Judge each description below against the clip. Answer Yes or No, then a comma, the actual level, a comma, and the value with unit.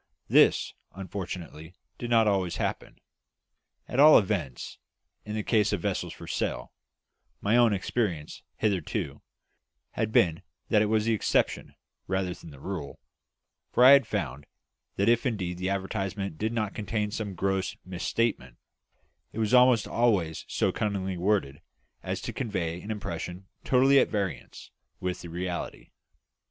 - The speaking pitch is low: Yes, low, 100 Hz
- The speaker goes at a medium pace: Yes, average, 145 wpm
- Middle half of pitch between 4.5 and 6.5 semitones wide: No, average, 3.7 semitones